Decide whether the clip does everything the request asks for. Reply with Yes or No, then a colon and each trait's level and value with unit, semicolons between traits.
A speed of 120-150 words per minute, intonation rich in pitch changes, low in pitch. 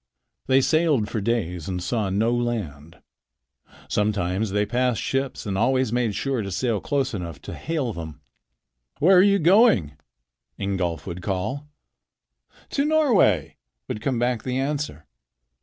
Yes: average, 140 wpm; wide, 6.2 semitones; low, 115 Hz